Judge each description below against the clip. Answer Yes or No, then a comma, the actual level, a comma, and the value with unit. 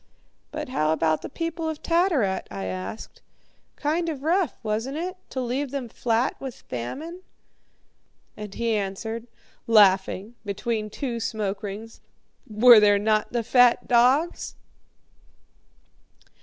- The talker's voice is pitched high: Yes, high, 230 Hz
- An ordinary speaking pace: No, slow, 125 wpm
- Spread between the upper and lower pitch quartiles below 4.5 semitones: No, average, 5.2 semitones